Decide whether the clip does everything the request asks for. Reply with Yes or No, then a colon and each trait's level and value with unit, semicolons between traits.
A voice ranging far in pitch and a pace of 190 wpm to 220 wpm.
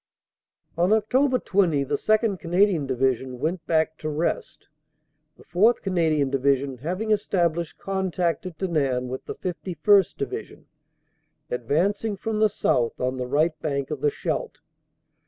No: wide, 5.9 semitones; slow, 135 wpm